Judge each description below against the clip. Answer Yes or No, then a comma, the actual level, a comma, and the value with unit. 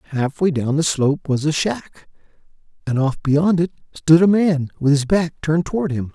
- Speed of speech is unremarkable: Yes, average, 195 wpm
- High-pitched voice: No, medium, 155 Hz